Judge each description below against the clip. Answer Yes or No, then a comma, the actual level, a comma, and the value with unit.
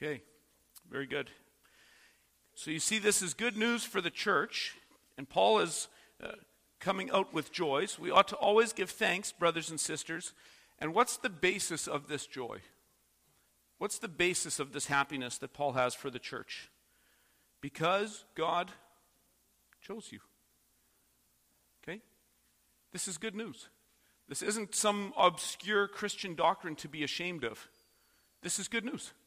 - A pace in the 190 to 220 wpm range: No, average, 150 wpm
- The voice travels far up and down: Yes, wide, 5.9 semitones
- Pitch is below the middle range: No, medium, 175 Hz